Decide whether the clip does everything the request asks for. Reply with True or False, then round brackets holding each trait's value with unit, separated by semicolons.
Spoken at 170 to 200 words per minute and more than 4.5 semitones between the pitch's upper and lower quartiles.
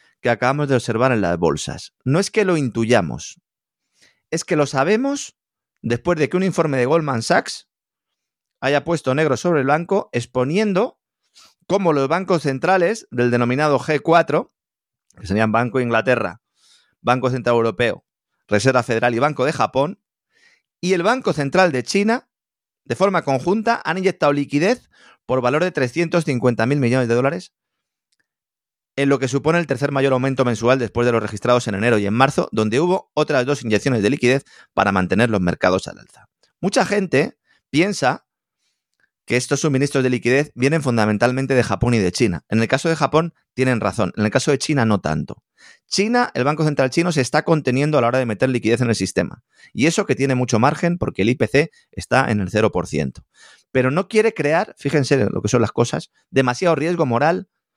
True (185 wpm; 5.3 semitones)